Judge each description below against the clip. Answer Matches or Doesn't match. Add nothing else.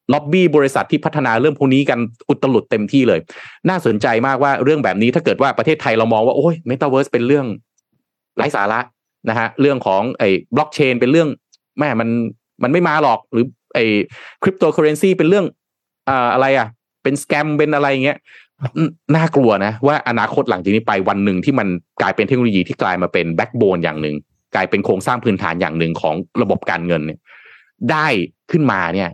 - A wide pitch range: Matches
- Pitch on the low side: Matches